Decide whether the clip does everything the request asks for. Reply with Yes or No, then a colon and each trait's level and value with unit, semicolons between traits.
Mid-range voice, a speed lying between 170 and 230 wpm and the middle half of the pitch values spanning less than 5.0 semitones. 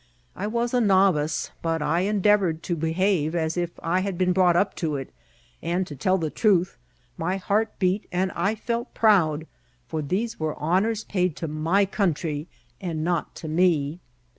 Yes: medium, 180 Hz; average, 175 wpm; average, 3.6 semitones